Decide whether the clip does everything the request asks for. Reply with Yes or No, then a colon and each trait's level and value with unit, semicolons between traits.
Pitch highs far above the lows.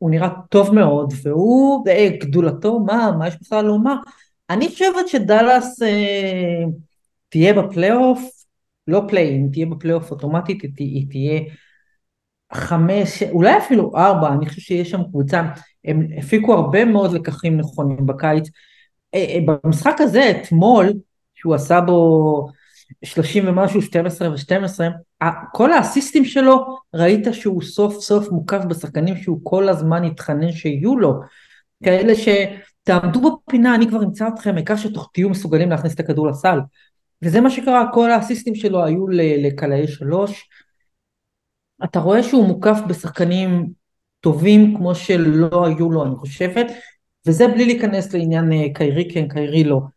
No: average, 4.8 semitones